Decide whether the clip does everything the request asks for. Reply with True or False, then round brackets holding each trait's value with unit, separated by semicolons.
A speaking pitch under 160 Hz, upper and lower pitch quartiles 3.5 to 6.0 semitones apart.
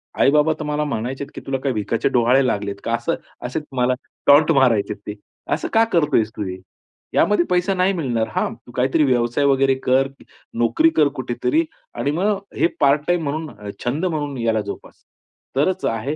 True (135 Hz; 4.6 semitones)